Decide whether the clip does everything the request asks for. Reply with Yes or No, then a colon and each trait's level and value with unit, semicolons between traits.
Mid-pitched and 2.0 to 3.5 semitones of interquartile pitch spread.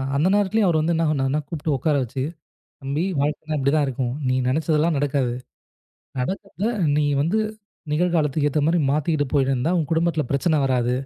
Yes: medium, 150 Hz; average, 3.2 semitones